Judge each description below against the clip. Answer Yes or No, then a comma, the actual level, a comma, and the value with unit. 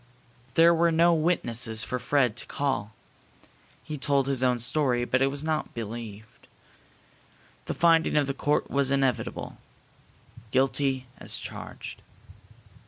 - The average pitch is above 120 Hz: Yes, low, 135 Hz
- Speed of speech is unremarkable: No, slow, 130 wpm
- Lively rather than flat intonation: No, average, 3.7 semitones